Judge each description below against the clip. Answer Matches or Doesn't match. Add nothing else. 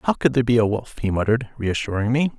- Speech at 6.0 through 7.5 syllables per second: Matches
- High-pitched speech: Doesn't match